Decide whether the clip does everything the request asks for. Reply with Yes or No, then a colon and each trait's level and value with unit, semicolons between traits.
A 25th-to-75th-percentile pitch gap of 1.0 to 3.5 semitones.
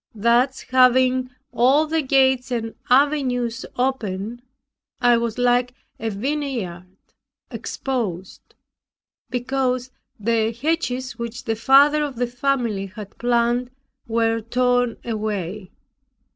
Yes: narrow, 2.4 semitones